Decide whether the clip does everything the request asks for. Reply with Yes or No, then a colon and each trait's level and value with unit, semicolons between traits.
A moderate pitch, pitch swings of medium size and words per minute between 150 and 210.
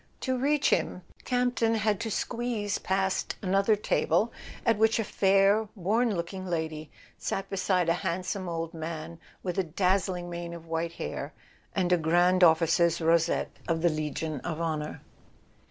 Yes: medium, 180 Hz; average, 3.5 semitones; average, 160 wpm